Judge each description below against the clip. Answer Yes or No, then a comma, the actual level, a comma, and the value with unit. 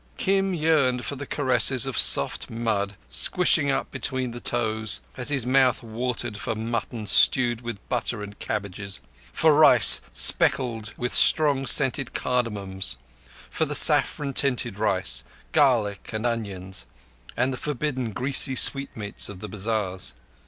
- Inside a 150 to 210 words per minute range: No, average, 140 wpm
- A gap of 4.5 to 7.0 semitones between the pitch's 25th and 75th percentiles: No, average, 4.1 semitones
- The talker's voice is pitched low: Yes, low, 120 Hz